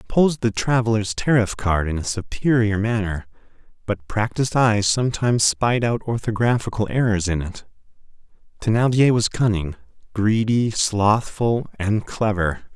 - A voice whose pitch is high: No, low, 110 Hz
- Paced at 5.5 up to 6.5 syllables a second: No, 4.9 syllables/s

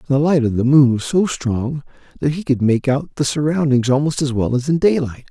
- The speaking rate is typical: No, fast, 235 wpm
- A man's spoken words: Yes, male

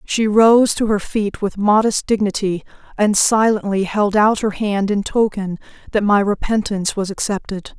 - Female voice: Yes, female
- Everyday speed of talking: Yes, average, 160 wpm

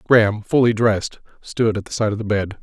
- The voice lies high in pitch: No, low, 110 Hz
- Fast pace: Yes, fast, 230 wpm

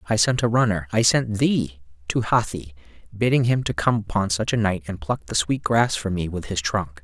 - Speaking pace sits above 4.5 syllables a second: Yes, 5.0 syllables/s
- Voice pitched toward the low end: Yes, low, 100 Hz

